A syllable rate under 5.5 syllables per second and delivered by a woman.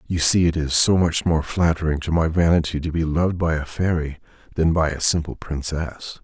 No: 5.2 syllables/s; male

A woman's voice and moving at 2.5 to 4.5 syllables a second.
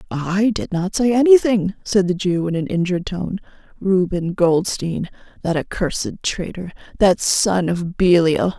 Yes: female; 4.3 syllables/s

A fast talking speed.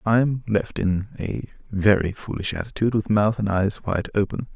No: average, 185 wpm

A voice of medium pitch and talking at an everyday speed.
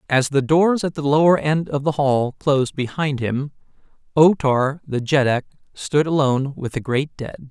Yes: medium, 145 Hz; average, 185 wpm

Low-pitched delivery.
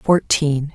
No: medium, 150 Hz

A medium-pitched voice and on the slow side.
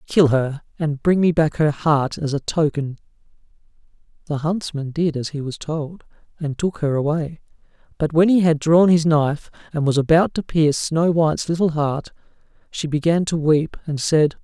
No: medium, 155 Hz; average, 185 wpm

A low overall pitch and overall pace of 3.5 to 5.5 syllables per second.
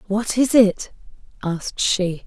No: high, 205 Hz; 3.8 syllables/s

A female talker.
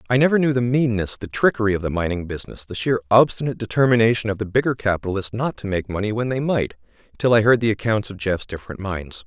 No: male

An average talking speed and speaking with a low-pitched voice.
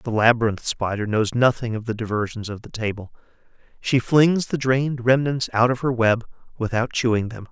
Yes: average, 185 wpm; low, 120 Hz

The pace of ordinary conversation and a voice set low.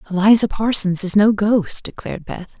No: average, 160 wpm; high, 205 Hz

